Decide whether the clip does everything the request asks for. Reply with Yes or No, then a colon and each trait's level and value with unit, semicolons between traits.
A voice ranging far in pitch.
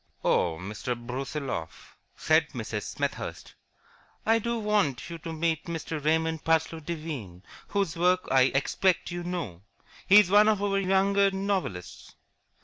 Yes: wide, 6.1 semitones